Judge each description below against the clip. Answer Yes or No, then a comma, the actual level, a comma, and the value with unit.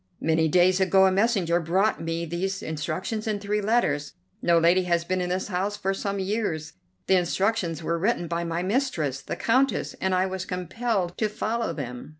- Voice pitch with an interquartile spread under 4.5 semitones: Yes, average, 3.3 semitones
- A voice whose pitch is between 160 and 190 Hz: Yes, medium, 185 Hz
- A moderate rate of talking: Yes, average, 185 wpm